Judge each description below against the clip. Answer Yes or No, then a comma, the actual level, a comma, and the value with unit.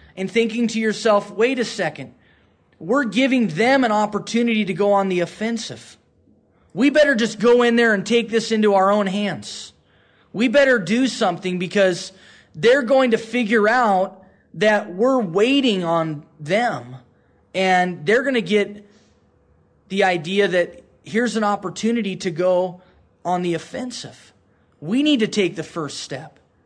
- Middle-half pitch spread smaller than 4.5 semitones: No, average, 4.9 semitones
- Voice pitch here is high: Yes, high, 200 Hz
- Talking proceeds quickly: No, average, 155 wpm